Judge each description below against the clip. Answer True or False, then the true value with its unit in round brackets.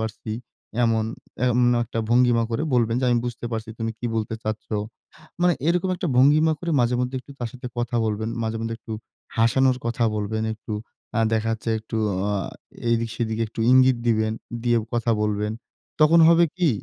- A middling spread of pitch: False (2.3 semitones)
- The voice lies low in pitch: True (115 Hz)